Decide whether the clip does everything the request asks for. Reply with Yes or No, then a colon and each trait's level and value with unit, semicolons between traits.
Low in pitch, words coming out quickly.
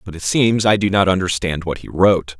Yes: very low, 95 Hz; fast, 250 wpm